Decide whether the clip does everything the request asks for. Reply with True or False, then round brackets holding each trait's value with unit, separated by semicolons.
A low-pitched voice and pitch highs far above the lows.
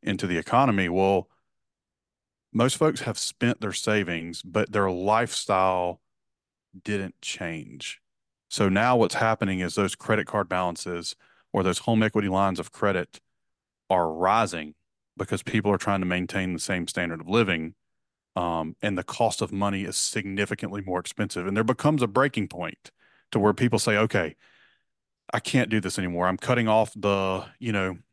False (100 Hz; 3.3 semitones)